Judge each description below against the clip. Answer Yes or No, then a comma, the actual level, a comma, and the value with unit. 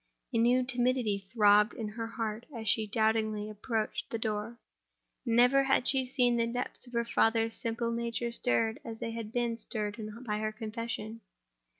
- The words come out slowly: No, average, 170 wpm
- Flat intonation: Yes, narrow, 1.7 semitones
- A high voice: Yes, high, 230 Hz